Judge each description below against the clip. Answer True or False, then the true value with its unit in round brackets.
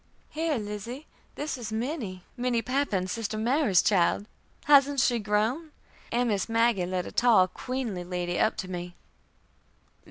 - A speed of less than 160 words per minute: True (145 wpm)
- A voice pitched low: False (225 Hz)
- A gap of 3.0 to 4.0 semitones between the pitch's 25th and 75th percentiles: False (5.3 semitones)